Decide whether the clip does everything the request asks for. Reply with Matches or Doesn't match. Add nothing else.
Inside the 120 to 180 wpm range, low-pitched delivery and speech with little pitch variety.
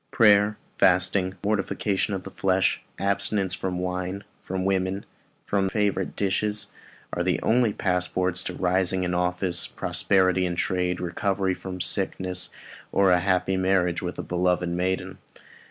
Matches